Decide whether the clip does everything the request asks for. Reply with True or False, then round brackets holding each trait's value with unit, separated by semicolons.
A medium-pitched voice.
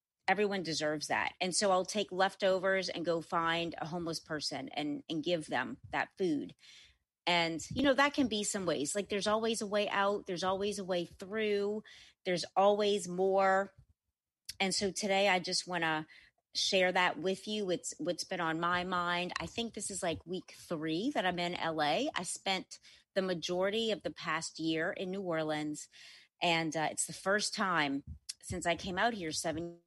True (180 Hz)